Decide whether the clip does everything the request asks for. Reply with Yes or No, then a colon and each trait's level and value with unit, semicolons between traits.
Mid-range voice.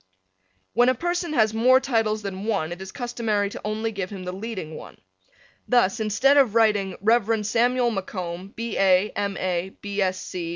No: high, 215 Hz